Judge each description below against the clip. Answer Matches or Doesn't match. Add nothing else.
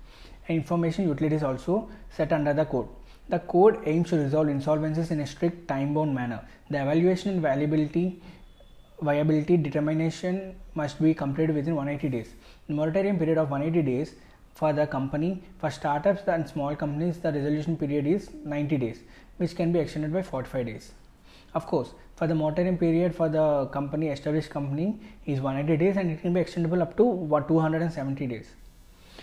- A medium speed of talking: Matches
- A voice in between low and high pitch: Matches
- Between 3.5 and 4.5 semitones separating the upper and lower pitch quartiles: Doesn't match